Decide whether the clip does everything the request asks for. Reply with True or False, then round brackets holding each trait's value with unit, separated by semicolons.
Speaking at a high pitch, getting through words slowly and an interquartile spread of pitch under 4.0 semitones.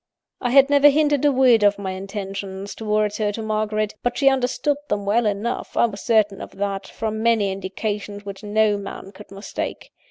False (210 Hz; 190 wpm; 2.9 semitones)